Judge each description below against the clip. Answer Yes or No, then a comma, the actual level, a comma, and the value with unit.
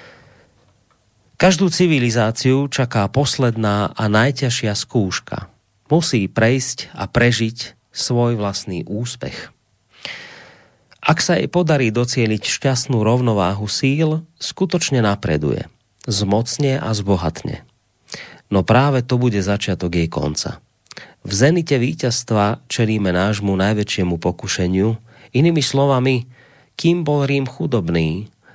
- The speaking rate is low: Yes, slow, 100 wpm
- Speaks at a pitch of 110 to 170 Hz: Yes, low, 120 Hz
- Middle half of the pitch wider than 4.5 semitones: Yes, average, 5.0 semitones